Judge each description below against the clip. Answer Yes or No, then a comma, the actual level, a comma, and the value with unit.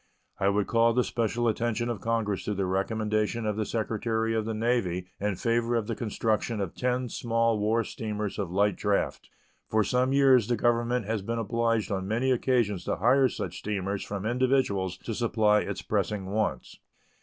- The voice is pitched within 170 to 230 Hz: No, low, 110 Hz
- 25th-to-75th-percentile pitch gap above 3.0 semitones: No, narrow, 2.4 semitones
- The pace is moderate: Yes, average, 180 wpm